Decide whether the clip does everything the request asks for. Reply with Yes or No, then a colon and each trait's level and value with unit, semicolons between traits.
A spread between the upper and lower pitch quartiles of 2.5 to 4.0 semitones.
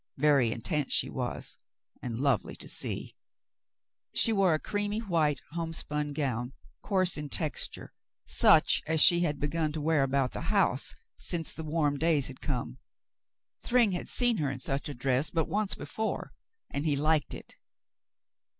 Yes: average, 3.5 semitones